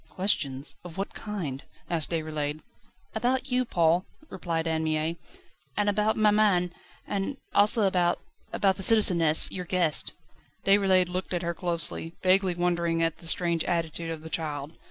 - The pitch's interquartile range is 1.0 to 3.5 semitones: Yes, average, 3.2 semitones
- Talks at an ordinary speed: Yes, average, 150 wpm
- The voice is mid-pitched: Yes, medium, 175 Hz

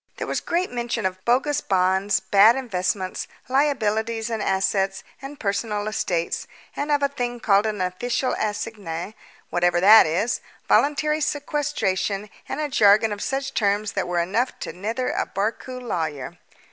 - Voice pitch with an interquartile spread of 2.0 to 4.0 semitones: No, average, 4.8 semitones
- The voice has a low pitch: No, high, 215 Hz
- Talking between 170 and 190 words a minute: No, average, 150 wpm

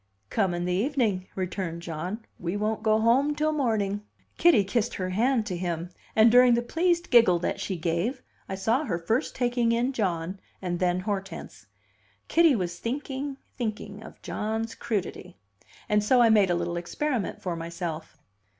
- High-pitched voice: Yes, high, 210 Hz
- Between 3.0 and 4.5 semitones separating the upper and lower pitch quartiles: No, average, 5.3 semitones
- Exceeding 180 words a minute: No, average, 170 wpm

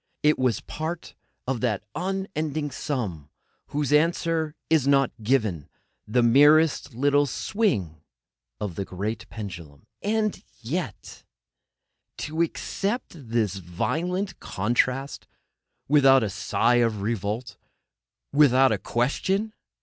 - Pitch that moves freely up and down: Yes, wide, 6.6 semitones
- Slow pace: Yes, slow, 105 wpm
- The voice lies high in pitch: No, low, 135 Hz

